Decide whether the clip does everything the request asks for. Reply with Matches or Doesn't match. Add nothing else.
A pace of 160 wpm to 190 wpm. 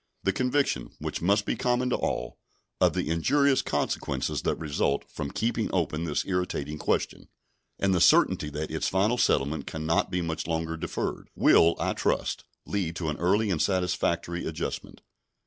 Matches